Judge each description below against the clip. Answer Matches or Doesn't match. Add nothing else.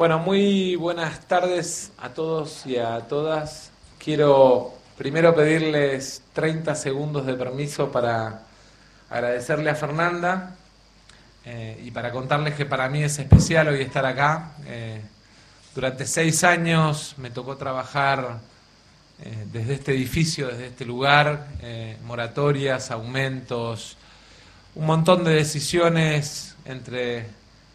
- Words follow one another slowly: Matches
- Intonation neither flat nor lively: Matches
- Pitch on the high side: Doesn't match